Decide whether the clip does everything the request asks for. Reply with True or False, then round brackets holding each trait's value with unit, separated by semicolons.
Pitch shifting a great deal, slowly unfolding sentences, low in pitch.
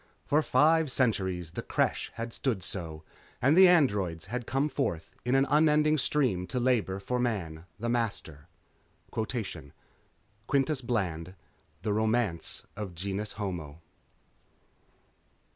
True (6.3 semitones; 120 wpm; 110 Hz)